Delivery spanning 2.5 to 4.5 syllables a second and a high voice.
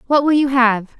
No: 5.0 syllables/s; very high, 260 Hz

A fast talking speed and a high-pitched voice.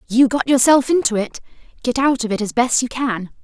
Yes: fast, 225 wpm; high, 245 Hz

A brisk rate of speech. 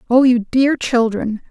No: average, 160 wpm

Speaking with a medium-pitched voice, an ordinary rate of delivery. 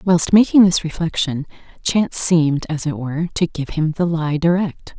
Yes: medium, 165 Hz; average, 180 wpm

